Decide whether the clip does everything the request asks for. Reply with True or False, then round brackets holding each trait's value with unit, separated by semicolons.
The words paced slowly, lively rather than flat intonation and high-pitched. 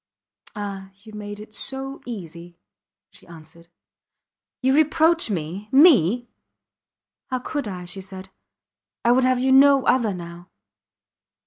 True (125 wpm; 6.6 semitones; 210 Hz)